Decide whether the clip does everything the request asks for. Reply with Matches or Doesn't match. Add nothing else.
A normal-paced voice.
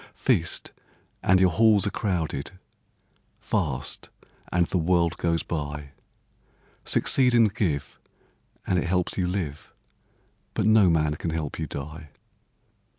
Doesn't match